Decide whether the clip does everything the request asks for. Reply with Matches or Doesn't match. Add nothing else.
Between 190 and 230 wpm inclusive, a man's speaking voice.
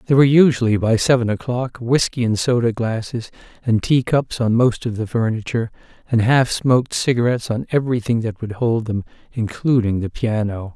Doesn't match